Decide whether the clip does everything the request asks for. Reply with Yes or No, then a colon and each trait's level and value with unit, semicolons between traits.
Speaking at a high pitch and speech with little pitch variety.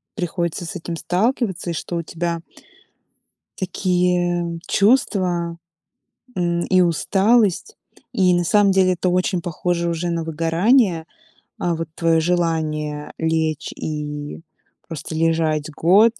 No: medium, 170 Hz; narrow, 2.1 semitones